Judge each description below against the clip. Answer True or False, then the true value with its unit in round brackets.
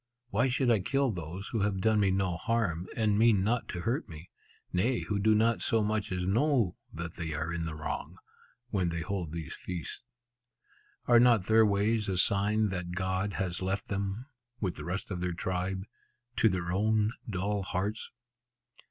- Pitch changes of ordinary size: True (3.5 semitones)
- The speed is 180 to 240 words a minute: True (185 wpm)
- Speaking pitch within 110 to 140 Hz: False (100 Hz)